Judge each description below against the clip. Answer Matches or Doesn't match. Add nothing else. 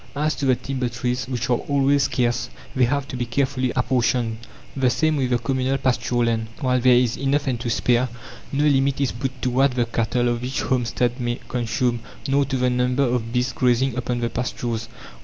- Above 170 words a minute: Matches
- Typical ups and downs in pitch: Doesn't match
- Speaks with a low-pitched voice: Matches